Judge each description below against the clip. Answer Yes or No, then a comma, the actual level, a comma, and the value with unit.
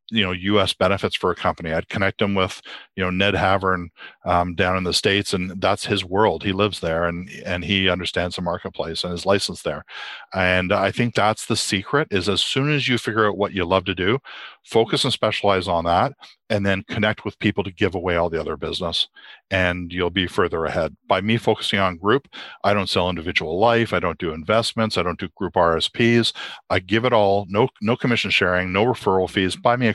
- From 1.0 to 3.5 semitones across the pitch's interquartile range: Yes, average, 2.8 semitones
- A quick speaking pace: Yes, fast, 220 wpm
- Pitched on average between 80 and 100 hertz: Yes, very low, 95 Hz